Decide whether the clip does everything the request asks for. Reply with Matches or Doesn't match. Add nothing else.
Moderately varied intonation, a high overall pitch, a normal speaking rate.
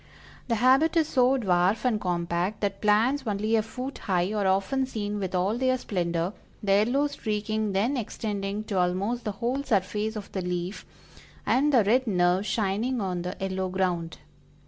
Matches